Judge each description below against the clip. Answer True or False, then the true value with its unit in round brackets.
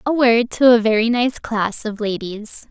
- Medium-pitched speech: False (230 Hz)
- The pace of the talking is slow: False (200 wpm)